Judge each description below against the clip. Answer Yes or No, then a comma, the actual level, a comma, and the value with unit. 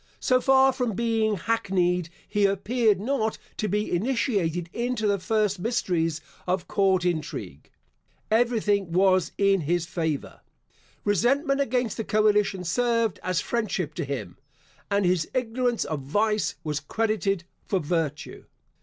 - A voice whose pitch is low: No, high, 200 Hz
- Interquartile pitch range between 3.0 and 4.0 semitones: No, average, 4.5 semitones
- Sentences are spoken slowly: Yes, slow, 130 wpm